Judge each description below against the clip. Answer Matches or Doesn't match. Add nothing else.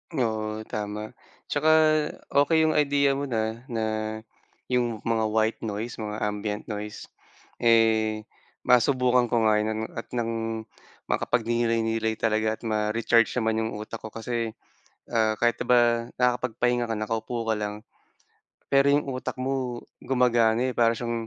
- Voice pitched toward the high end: Doesn't match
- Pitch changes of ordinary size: Doesn't match